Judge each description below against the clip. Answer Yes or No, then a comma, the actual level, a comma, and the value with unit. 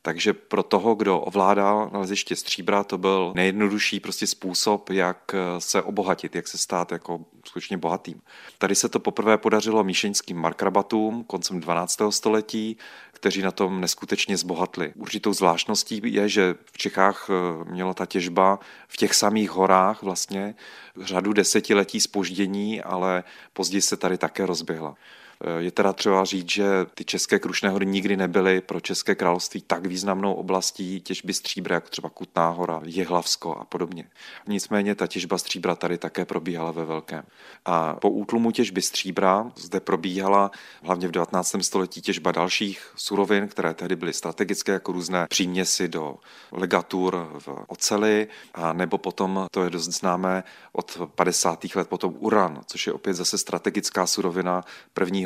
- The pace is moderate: Yes, average, 150 wpm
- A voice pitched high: No, very low, 95 Hz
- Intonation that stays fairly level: Yes, narrow, 2.0 semitones